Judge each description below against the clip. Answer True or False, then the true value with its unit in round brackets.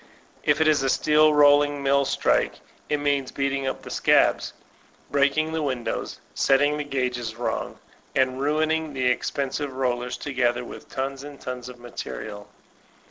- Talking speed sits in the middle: True (150 wpm)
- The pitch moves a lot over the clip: False (2.4 semitones)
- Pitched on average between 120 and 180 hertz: True (140 Hz)